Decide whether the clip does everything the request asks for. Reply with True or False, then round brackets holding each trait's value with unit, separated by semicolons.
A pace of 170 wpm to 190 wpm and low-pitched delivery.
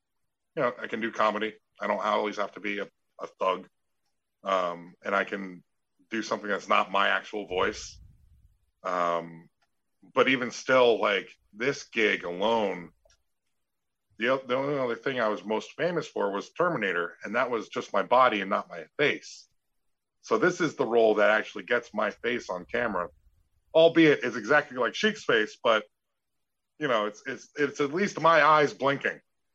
True (175 wpm; 110 Hz)